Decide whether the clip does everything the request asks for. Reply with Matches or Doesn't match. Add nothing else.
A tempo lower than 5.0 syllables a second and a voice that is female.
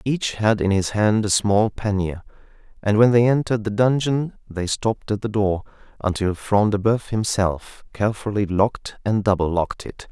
Doesn't match